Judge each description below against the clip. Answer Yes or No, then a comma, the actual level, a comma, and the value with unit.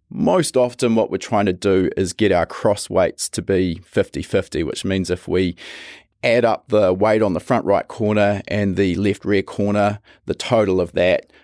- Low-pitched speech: Yes, low, 100 Hz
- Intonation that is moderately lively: No, narrow, 1.8 semitones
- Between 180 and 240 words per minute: Yes, average, 200 wpm